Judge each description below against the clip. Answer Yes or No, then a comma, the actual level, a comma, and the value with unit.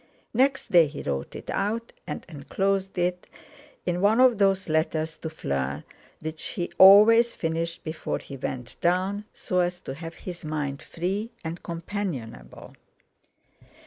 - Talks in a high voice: No, medium, 175 Hz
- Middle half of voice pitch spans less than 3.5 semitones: No, average, 4.0 semitones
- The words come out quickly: No, average, 145 wpm